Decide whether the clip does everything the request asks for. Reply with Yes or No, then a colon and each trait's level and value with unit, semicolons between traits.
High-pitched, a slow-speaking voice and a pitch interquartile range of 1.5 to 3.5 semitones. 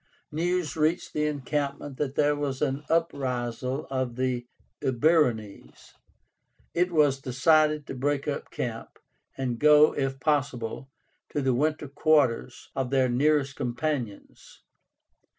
No: medium, 140 Hz; slow, 120 wpm; average, 2.9 semitones